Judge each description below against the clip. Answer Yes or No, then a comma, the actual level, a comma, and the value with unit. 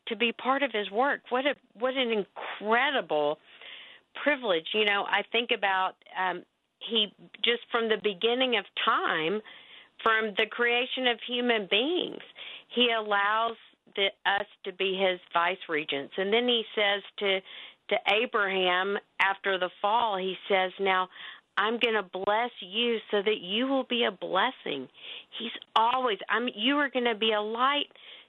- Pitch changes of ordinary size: Yes, average, 3.6 semitones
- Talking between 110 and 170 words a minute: Yes, average, 160 wpm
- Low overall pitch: No, high, 220 Hz